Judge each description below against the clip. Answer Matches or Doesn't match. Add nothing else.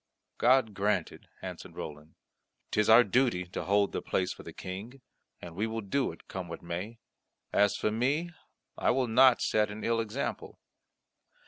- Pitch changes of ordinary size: Matches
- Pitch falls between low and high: Doesn't match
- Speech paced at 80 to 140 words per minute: Doesn't match